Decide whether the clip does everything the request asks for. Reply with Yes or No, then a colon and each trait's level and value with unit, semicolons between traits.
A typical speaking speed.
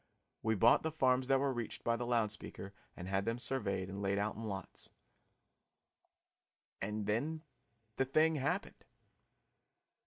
Yes: average, 150 wpm